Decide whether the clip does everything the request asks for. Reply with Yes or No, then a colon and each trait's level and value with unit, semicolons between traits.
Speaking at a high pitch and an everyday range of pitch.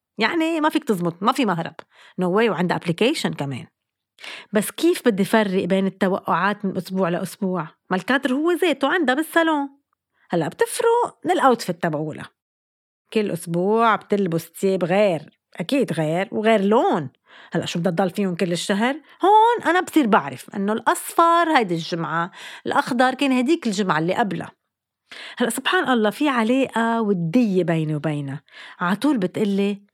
No: high, 210 Hz; wide, 7.1 semitones